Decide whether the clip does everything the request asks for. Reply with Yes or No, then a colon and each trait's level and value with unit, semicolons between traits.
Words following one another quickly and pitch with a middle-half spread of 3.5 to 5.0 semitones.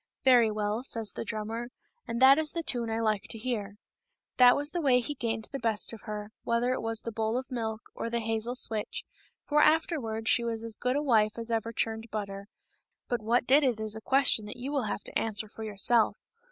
No: fast, 235 wpm; narrow, 2.5 semitones